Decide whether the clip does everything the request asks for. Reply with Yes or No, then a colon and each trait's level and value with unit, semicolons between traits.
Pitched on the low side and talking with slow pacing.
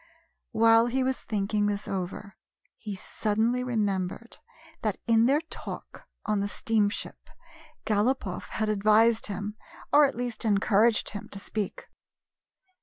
No: high, 215 Hz; slow, 125 wpm